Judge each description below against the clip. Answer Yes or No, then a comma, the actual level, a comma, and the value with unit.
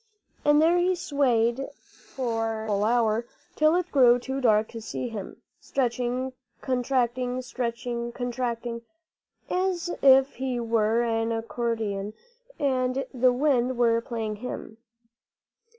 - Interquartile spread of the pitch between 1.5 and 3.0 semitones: Yes, narrow, 2.4 semitones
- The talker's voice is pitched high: Yes, high, 245 Hz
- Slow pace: Yes, slow, 120 wpm